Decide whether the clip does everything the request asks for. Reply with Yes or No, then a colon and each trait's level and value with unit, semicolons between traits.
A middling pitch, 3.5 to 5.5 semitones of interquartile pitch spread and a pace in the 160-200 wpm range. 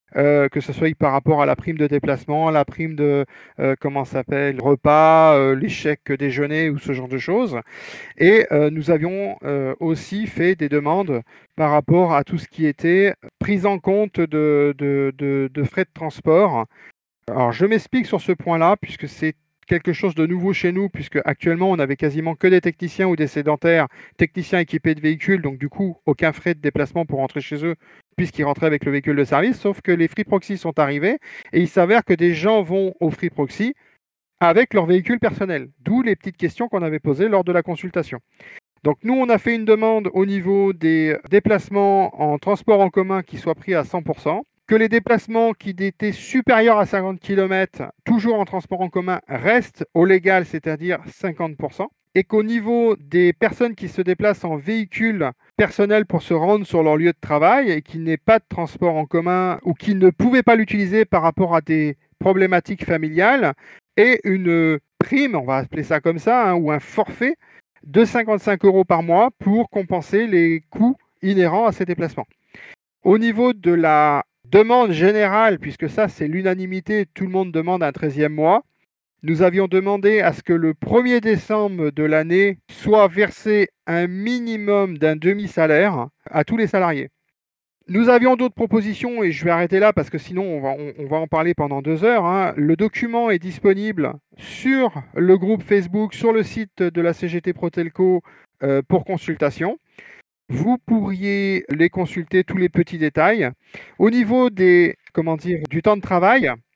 Yes: medium, 180 Hz; average, 4.6 semitones; average, 185 wpm